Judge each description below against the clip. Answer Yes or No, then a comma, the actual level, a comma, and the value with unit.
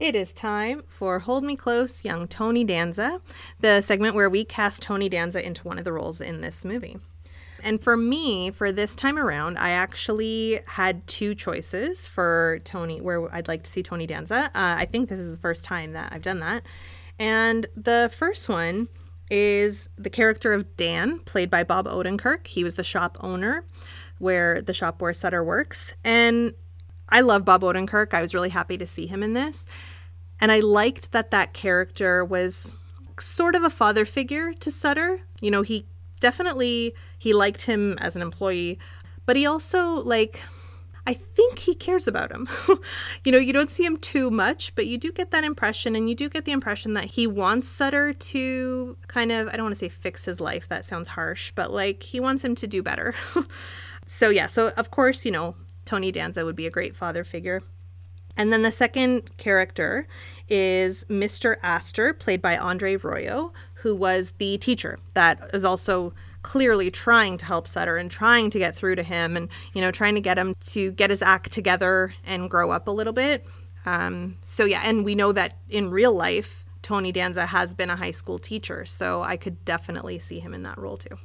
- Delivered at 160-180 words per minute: No, average, 200 wpm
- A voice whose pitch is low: No, high, 190 Hz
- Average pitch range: No, wide, 5.7 semitones